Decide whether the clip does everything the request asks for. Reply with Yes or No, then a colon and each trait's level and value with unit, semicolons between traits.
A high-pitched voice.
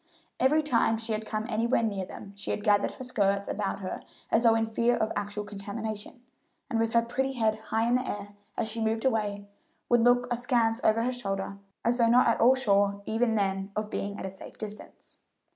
Yes: high, 225 Hz